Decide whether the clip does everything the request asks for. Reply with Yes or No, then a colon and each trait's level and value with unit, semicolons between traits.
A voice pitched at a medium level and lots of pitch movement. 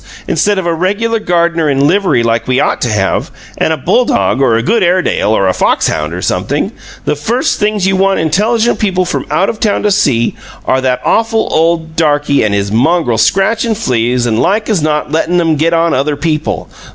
Yes: medium, 165 Hz; wide, 7.1 semitones